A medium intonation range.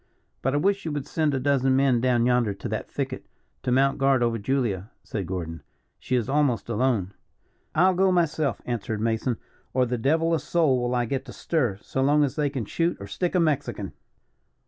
Yes: average, 4.2 semitones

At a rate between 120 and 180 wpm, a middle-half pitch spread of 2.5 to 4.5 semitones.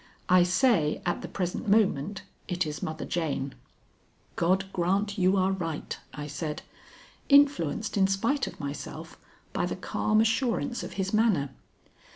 No: average, 145 wpm; average, 5.2 semitones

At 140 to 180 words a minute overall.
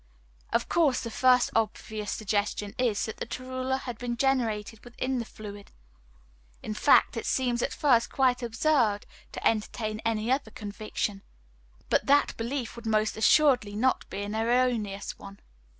Yes: average, 150 wpm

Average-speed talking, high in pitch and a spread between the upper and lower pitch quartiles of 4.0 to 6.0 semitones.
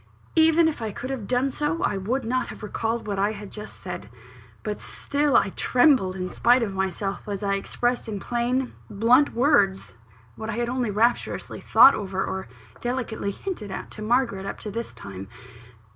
Yes: average, 185 wpm; high, 225 Hz; average, 4.3 semitones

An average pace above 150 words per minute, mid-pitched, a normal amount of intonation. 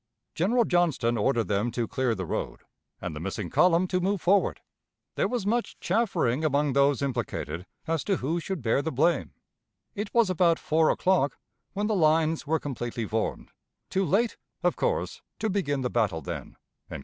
No: average, 175 wpm; medium, 155 Hz; wide, 7.7 semitones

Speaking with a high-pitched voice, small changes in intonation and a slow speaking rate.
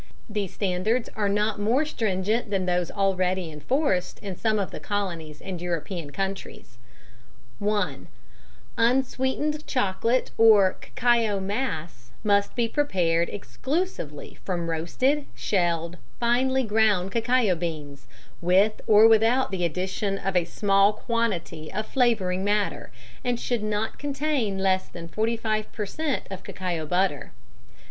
No: high, 200 Hz; average, 4.3 semitones; slow, 125 wpm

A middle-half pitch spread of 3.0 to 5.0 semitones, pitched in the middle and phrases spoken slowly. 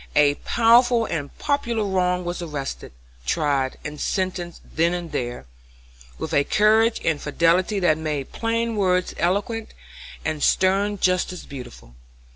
No: wide, 5.6 semitones; medium, 180 Hz; slow, 130 wpm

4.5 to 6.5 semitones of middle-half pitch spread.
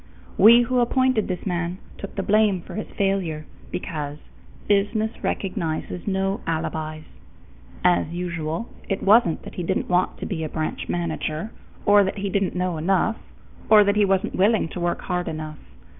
No: average, 3.5 semitones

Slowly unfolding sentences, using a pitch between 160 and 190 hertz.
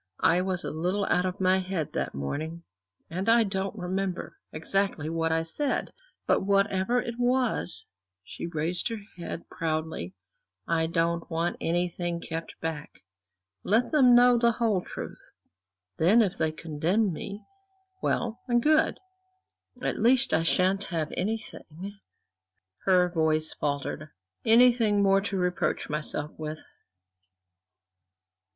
Yes: slow, 130 wpm; medium, 185 Hz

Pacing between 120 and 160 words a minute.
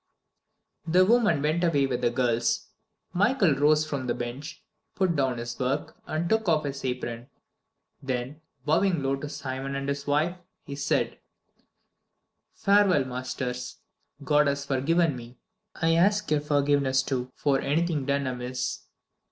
Yes: average, 145 wpm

